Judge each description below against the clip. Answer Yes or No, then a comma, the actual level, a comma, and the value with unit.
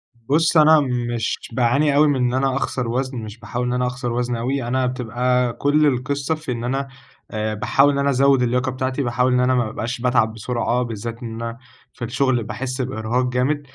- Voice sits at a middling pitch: No, low, 125 Hz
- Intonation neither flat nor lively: No, narrow, 2.2 semitones